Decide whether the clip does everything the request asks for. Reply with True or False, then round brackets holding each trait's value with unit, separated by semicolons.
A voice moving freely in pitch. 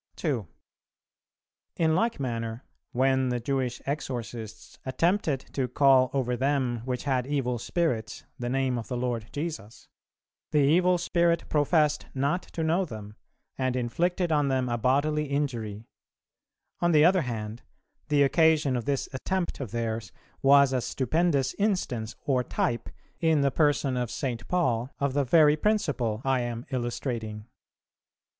False (4.0 semitones)